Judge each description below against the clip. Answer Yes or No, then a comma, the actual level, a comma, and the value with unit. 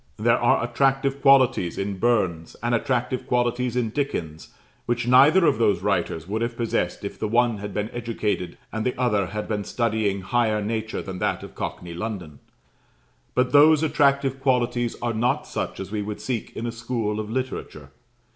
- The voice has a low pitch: Yes, low, 115 Hz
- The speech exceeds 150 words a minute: Yes, average, 175 wpm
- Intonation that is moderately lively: Yes, average, 3.4 semitones